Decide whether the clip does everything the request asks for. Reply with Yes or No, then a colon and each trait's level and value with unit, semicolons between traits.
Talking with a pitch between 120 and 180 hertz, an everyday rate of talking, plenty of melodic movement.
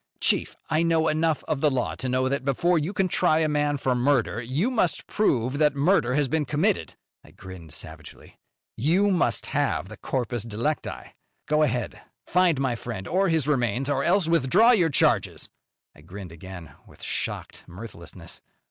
Yes: medium, 140 Hz; average, 175 wpm; wide, 5.7 semitones